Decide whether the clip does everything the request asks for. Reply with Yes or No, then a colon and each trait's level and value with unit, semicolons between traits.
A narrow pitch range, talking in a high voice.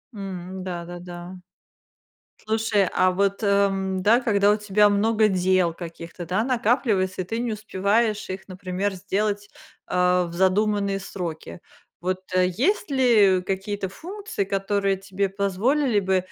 Yes: narrow, 2.3 semitones; high, 195 Hz